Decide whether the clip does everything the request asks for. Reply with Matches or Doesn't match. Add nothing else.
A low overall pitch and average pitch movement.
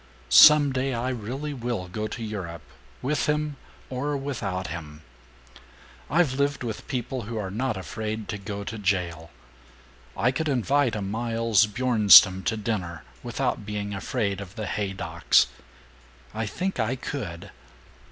Matches